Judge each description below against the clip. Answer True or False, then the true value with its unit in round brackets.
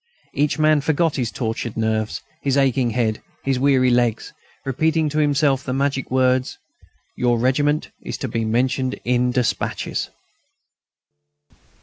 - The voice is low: True (130 Hz)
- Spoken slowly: True (130 wpm)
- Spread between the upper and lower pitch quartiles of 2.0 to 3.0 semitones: True (2.7 semitones)